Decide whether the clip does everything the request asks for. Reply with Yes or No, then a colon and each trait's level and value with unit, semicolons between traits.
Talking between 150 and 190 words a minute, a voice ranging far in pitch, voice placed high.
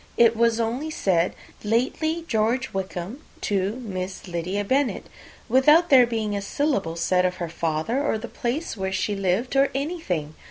Yes: average, 165 wpm; wide, 5.9 semitones; high, 220 Hz